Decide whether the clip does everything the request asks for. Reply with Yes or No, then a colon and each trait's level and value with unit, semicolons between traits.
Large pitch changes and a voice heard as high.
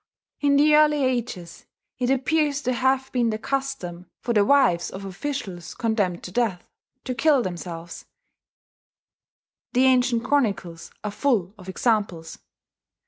Yes: wide, 6.6 semitones; high, 235 Hz